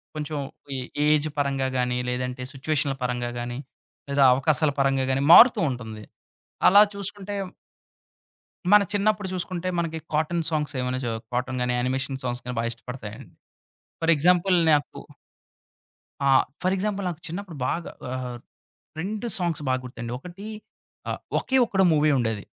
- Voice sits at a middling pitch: Yes, medium, 145 Hz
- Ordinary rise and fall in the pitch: No, wide, 5.9 semitones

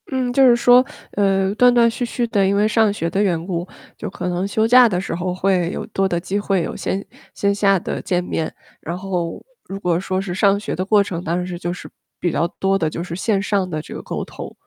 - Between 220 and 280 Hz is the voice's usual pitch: No, high, 195 Hz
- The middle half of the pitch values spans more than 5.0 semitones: No, average, 2.7 semitones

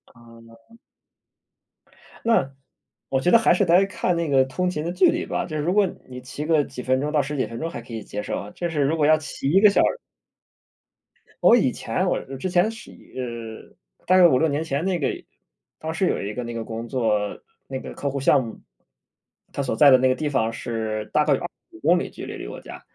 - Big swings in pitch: Yes, wide, 6.1 semitones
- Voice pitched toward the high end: No, medium, 140 Hz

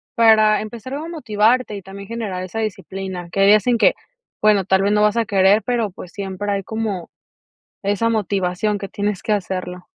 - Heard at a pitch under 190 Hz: No, high, 205 Hz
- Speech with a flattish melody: Yes, narrow, 2.3 semitones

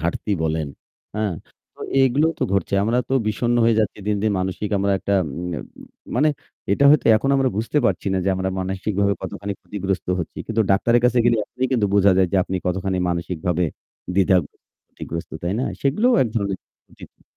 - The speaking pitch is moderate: No, low, 100 Hz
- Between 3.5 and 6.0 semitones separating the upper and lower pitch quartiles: Yes, average, 4.1 semitones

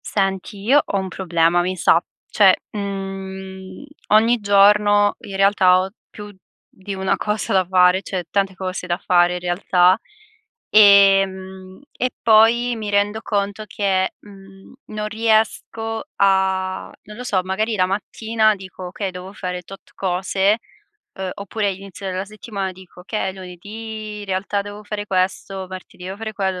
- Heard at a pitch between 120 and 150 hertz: No, high, 195 Hz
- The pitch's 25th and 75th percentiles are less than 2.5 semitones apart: Yes, narrow, 1.9 semitones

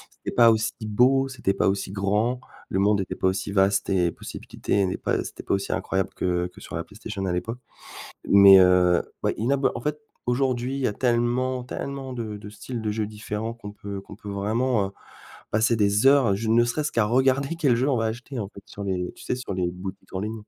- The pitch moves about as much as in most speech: Yes, average, 4.0 semitones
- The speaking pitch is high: No, low, 110 Hz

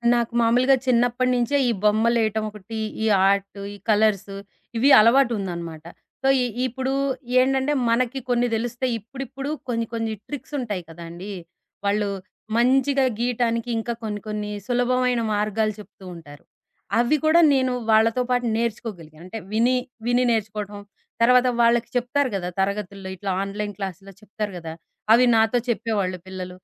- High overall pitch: Yes, high, 225 Hz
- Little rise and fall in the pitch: No, average, 3.5 semitones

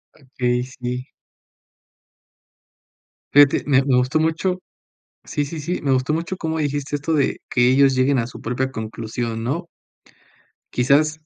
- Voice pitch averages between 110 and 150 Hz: Yes, low, 135 Hz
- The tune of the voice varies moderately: Yes, average, 3.4 semitones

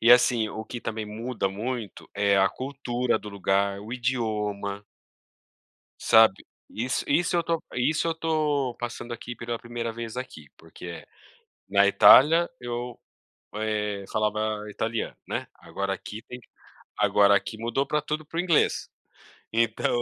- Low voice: Yes, low, 115 Hz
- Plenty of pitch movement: No, average, 3.3 semitones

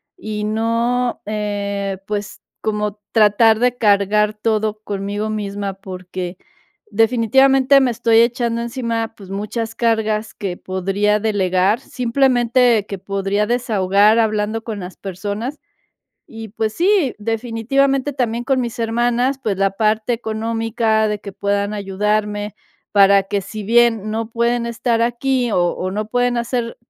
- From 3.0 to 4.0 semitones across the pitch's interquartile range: No, narrow, 2.5 semitones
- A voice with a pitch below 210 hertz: No, high, 220 Hz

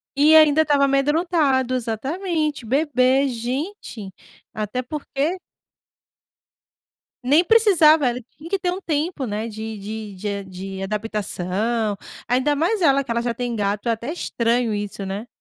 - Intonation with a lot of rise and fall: Yes, wide, 5.8 semitones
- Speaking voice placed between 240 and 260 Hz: Yes, very high, 255 Hz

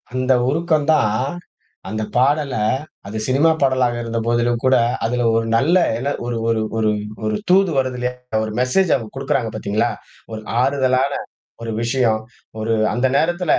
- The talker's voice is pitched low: Yes, low, 125 Hz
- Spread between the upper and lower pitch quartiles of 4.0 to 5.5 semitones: No, average, 3.3 semitones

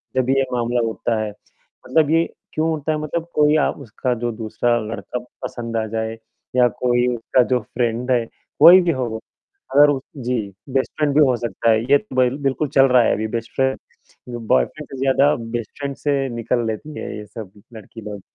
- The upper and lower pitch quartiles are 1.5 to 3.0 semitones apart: No, average, 3.7 semitones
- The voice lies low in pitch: Yes, low, 125 Hz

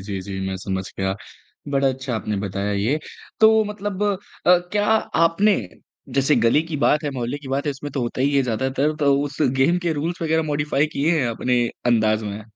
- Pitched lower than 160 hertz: Yes, medium, 140 Hz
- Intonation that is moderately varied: No, wide, 5.7 semitones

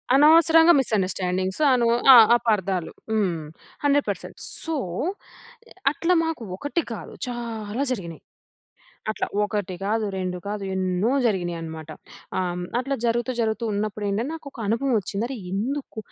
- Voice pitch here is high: Yes, high, 215 Hz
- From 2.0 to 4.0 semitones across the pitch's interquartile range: No, wide, 5.4 semitones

